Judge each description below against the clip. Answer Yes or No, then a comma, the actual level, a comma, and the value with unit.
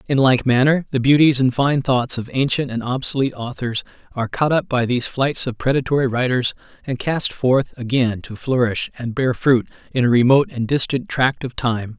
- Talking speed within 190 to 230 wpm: Yes, average, 195 wpm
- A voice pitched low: Yes, low, 130 Hz